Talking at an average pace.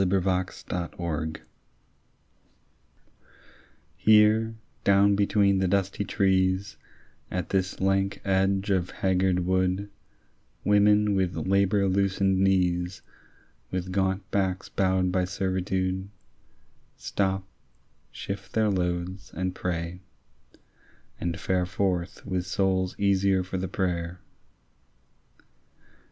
No: slow, 95 wpm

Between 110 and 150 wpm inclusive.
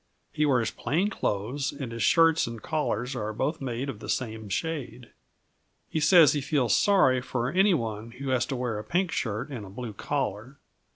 No: average, 190 wpm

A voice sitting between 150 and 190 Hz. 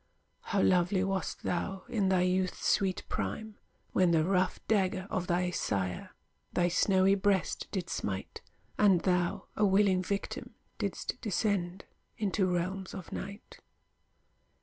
Yes: medium, 185 Hz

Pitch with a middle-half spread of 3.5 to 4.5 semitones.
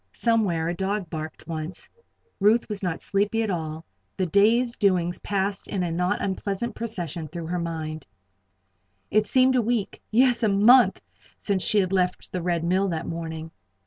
Yes: average, 4.0 semitones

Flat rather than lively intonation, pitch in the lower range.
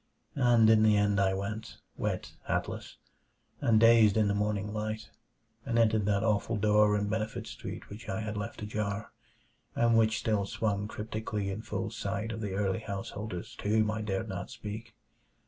Yes: narrow, 1.4 semitones; low, 105 Hz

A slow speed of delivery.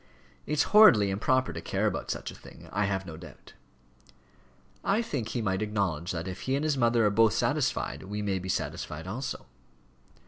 No: average, 185 wpm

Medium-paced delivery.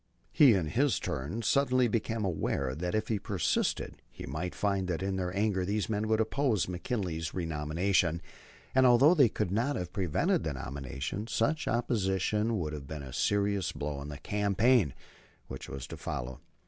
Yes: average, 175 wpm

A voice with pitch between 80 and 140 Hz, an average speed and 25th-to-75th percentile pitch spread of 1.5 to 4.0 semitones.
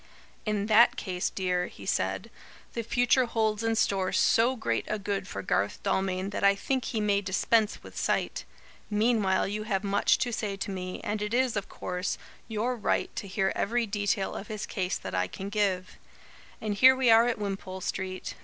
No: high, 205 Hz; average, 190 wpm; average, 2.8 semitones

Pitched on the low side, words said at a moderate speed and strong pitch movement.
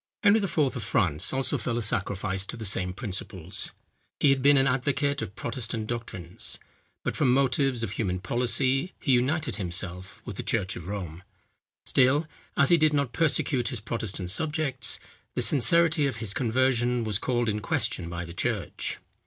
Yes: low, 120 Hz; average, 170 wpm; wide, 5.7 semitones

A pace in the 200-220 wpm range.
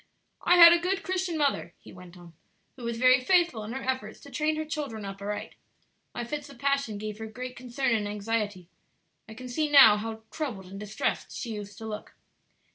Yes: fast, 205 wpm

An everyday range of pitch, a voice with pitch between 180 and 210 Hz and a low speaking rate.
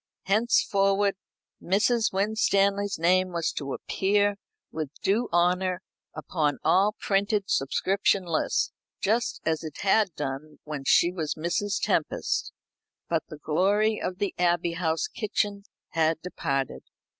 Yes: average, 4.0 semitones; medium, 185 Hz; slow, 120 wpm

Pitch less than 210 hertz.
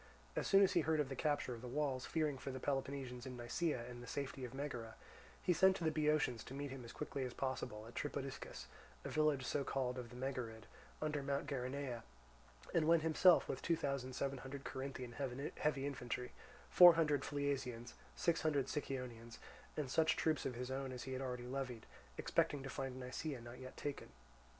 Yes: low, 135 Hz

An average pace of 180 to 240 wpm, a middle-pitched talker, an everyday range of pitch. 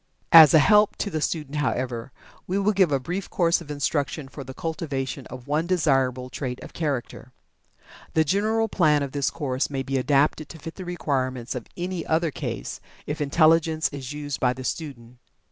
Yes: average, 185 wpm; medium, 150 Hz; average, 3.8 semitones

